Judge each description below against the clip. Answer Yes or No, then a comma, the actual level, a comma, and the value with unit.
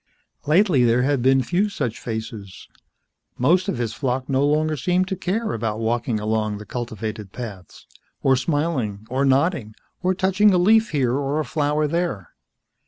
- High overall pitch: No, low, 135 Hz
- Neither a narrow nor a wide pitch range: No, wide, 6.9 semitones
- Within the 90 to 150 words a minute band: No, average, 165 wpm